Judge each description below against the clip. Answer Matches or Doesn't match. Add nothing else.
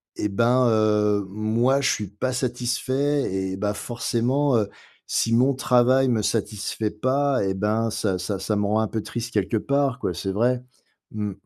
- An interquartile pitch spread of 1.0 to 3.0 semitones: Doesn't match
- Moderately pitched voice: Doesn't match